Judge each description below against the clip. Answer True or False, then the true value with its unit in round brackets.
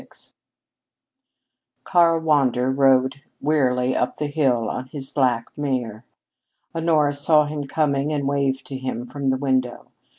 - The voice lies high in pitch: False (135 Hz)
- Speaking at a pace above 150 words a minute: False (135 wpm)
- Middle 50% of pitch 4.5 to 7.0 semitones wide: False (2.4 semitones)